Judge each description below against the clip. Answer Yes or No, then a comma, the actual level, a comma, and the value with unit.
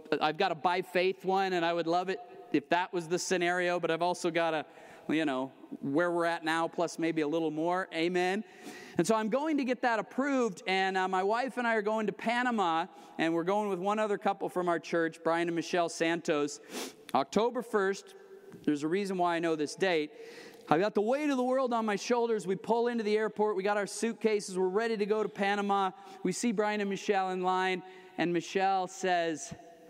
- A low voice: No, high, 190 Hz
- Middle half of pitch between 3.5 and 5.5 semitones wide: Yes, average, 4.1 semitones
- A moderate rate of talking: No, fast, 220 wpm